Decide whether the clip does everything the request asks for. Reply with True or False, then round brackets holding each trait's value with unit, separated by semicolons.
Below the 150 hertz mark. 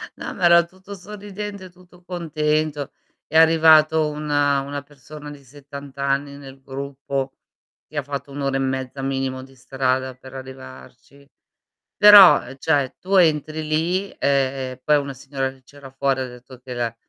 True (140 Hz)